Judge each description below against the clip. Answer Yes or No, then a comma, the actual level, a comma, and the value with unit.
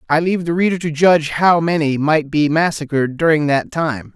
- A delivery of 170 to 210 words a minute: Yes, average, 200 wpm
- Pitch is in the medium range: Yes, medium, 155 Hz